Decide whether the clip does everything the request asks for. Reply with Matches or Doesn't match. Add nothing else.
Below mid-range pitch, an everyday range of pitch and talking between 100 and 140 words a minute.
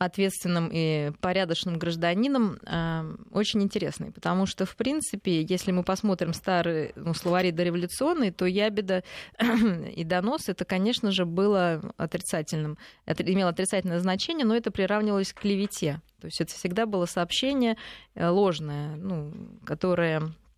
Doesn't match